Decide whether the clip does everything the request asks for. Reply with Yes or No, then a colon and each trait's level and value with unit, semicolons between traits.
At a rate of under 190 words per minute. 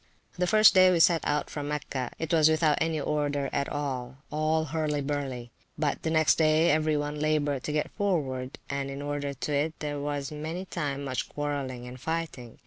No: average, 195 wpm